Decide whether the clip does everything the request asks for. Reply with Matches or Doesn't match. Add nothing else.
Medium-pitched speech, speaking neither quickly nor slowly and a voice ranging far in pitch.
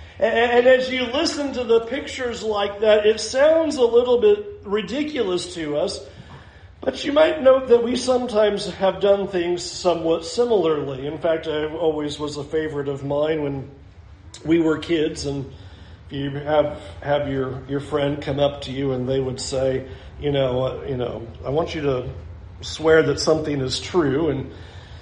Matches